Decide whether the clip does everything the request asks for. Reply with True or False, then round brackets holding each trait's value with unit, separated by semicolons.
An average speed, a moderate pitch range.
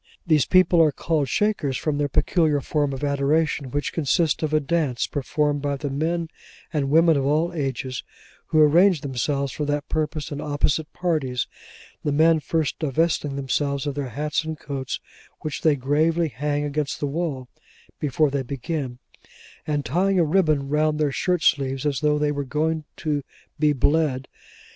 False (170 wpm; 2.2 semitones)